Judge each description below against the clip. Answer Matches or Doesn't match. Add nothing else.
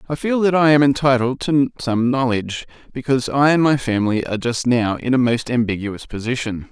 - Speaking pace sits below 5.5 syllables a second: Doesn't match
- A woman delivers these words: Doesn't match